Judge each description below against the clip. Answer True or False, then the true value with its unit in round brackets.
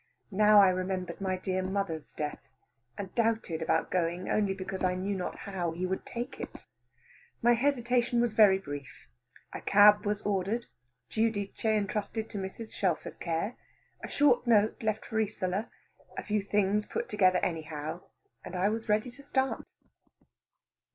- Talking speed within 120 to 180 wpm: True (155 wpm)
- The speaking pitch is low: False (200 Hz)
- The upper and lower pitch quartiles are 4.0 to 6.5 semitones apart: False (3.0 semitones)